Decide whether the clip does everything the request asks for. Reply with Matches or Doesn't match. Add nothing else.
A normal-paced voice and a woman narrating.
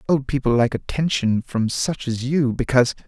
Doesn't match